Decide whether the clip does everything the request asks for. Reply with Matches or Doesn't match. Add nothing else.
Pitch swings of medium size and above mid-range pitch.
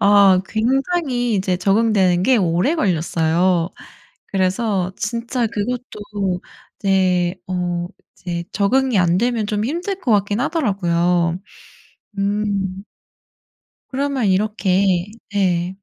Matches